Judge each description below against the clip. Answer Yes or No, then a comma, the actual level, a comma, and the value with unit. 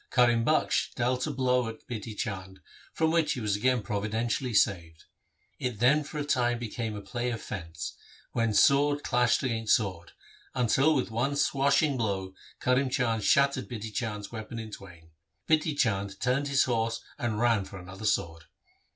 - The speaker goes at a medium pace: Yes, average, 170 wpm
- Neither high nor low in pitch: No, low, 115 Hz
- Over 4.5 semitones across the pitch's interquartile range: No, average, 3.9 semitones